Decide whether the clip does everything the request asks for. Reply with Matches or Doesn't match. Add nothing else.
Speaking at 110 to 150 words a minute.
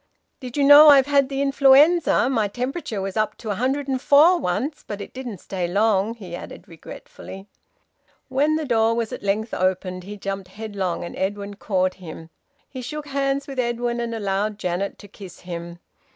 Doesn't match